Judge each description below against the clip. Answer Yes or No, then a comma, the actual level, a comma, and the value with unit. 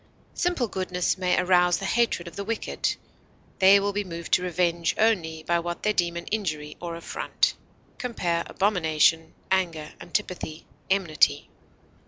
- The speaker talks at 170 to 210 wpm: No, average, 145 wpm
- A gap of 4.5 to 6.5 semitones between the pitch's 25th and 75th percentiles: No, average, 2.9 semitones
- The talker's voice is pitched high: No, medium, 180 Hz